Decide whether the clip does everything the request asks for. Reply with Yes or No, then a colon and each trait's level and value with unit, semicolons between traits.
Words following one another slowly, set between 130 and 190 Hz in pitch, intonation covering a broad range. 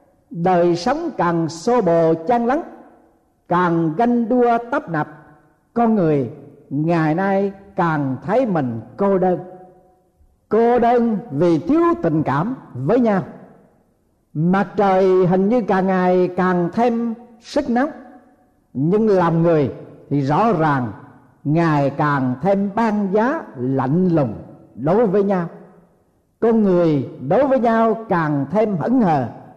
Yes: slow, 130 wpm; medium, 185 Hz; wide, 6.7 semitones